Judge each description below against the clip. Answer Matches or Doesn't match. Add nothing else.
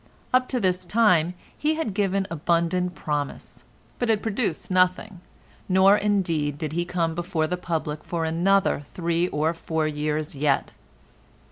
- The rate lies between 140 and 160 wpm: Matches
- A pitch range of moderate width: Matches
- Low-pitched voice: Doesn't match